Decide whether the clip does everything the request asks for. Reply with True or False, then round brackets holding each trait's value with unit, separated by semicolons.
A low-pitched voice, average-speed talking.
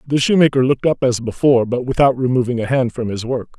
False (125 Hz; 235 wpm)